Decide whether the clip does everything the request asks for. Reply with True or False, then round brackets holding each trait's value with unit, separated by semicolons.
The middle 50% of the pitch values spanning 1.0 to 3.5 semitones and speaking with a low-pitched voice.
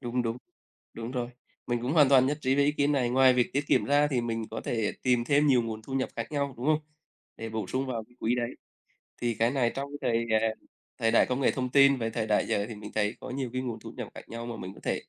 True (2.9 semitones; 125 Hz)